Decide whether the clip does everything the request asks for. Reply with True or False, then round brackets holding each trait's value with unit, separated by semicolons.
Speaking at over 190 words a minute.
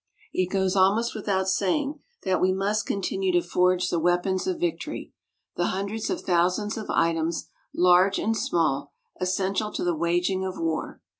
False (160 wpm)